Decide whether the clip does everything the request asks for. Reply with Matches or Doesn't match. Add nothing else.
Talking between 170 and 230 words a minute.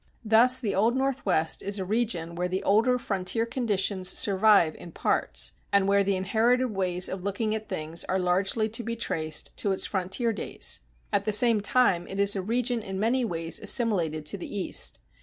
Matches